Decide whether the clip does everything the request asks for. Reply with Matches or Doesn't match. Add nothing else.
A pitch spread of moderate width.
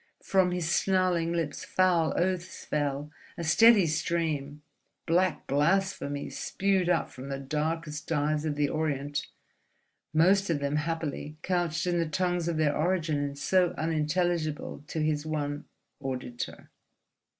Matches